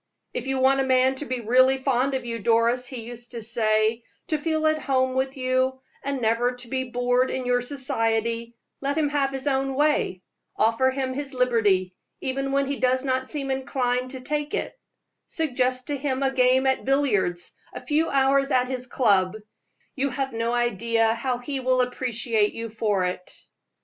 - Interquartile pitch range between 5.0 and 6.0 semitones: No, narrow, 2.5 semitones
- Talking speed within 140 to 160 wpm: No, average, 185 wpm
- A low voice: No, very high, 255 Hz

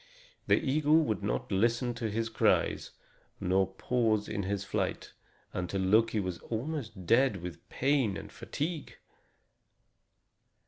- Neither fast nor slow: No, slow, 125 wpm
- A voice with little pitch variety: No, average, 4.8 semitones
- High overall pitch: No, low, 110 Hz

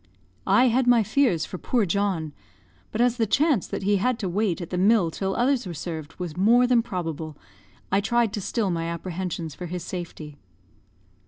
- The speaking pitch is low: No, high, 195 Hz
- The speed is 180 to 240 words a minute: Yes, average, 190 wpm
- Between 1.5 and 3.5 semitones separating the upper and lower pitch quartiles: No, wide, 5.4 semitones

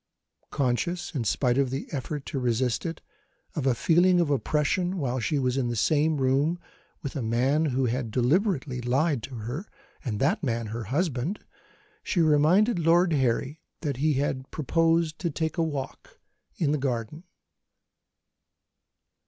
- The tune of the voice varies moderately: Yes, average, 4.4 semitones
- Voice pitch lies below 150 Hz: Yes, medium, 140 Hz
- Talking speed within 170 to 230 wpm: No, average, 155 wpm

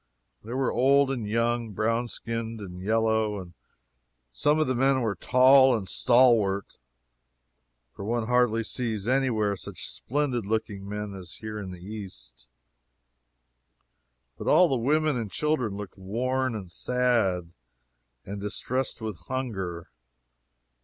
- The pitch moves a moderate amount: Yes, average, 4.1 semitones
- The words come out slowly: Yes, slow, 130 wpm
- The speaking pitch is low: Yes, low, 115 Hz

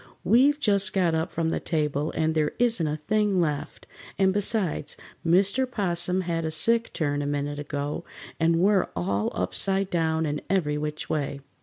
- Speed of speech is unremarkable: Yes, average, 170 wpm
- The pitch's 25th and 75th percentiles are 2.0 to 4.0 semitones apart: No, average, 4.7 semitones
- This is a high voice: No, medium, 165 Hz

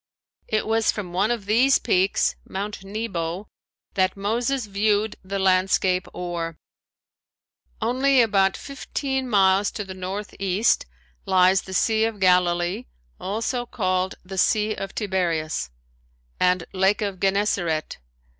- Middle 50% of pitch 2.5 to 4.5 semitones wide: Yes, average, 2.9 semitones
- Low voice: No, high, 195 Hz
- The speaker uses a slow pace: Yes, slow, 120 wpm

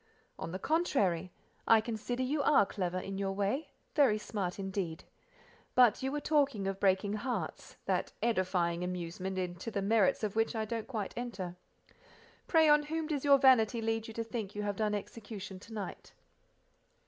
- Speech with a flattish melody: No, average, 4.2 semitones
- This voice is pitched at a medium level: No, high, 215 Hz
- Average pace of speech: Yes, average, 165 wpm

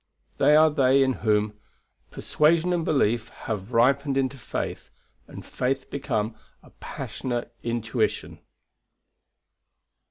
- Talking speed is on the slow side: Yes, slow, 105 wpm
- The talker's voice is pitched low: Yes, low, 130 Hz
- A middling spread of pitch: Yes, average, 3.6 semitones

